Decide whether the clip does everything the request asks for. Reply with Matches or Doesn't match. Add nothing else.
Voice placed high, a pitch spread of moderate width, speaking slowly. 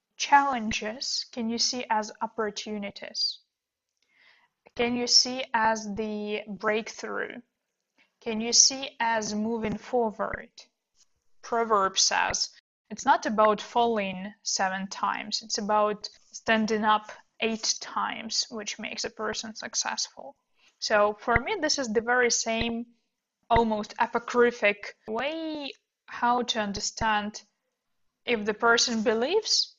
Doesn't match